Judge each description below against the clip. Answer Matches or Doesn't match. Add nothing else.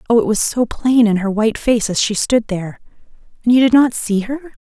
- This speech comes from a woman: Matches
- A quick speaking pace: Matches